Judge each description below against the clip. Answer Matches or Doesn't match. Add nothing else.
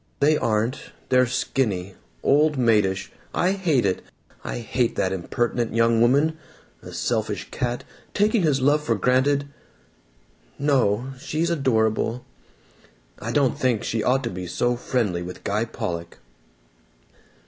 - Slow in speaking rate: Matches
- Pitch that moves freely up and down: Doesn't match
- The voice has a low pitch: Matches